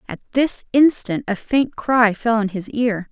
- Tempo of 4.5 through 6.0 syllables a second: No, 4.2 syllables/s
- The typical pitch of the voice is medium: No, high, 230 Hz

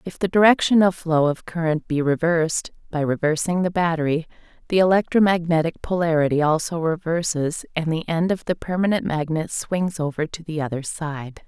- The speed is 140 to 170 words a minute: Yes, average, 160 wpm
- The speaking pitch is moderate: Yes, medium, 165 Hz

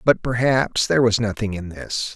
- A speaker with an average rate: Yes, average, 195 wpm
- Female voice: No, male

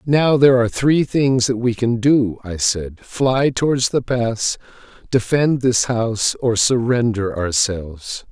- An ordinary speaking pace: Yes, average, 150 wpm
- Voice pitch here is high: No, low, 120 Hz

